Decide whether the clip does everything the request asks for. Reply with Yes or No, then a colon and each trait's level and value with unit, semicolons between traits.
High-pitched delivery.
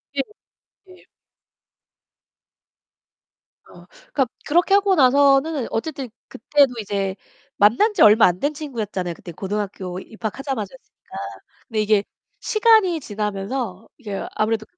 Yes: high, 230 Hz